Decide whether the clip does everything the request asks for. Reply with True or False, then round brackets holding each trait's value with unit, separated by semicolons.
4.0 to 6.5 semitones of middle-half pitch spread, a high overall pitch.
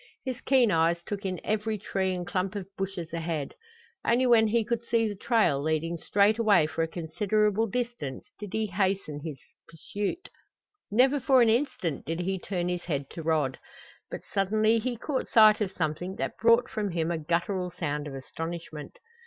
True (5.0 semitones; 195 Hz)